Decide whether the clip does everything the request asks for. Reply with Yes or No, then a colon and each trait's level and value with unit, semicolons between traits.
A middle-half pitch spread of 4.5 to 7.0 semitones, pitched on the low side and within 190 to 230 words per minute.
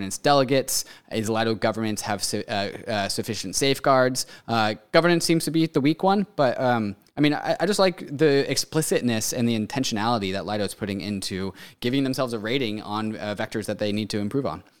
Yes: average, 4.9 semitones; low, 115 Hz; average, 200 wpm